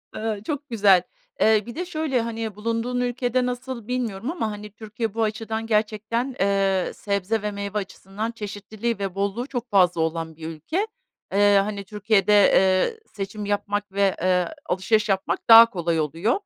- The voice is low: No, high, 210 Hz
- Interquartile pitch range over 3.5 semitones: No, average, 2.8 semitones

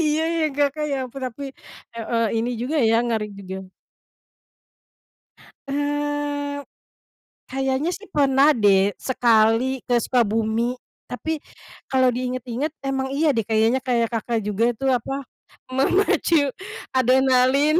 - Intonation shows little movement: No, average, 3.7 semitones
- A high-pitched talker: Yes, very high, 260 Hz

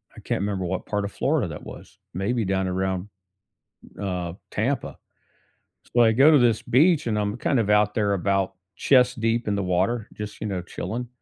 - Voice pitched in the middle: No, low, 105 Hz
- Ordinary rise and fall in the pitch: Yes, average, 3.7 semitones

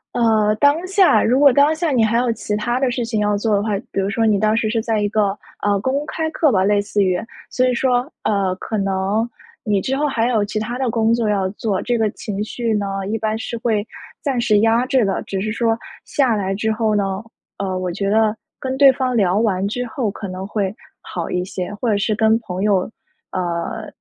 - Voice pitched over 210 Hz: Yes, high, 220 Hz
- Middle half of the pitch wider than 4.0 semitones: No, average, 3.1 semitones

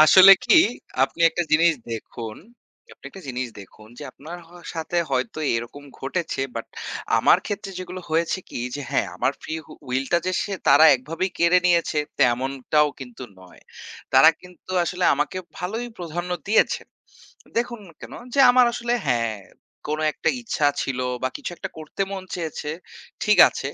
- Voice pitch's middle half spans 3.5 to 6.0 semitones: Yes, wide, 5.5 semitones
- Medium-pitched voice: Yes, medium, 160 Hz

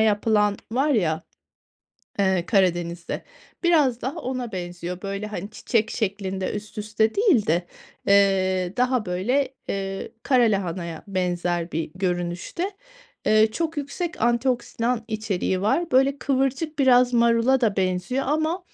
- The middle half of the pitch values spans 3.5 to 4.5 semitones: No, wide, 5.6 semitones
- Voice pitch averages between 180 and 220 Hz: Yes, high, 215 Hz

